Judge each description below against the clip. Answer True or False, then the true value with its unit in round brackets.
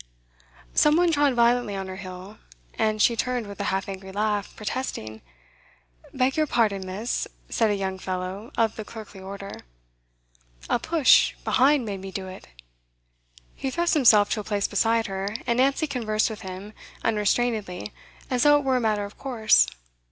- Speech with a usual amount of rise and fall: True (4.1 semitones)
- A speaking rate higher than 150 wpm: True (170 wpm)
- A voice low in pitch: False (215 Hz)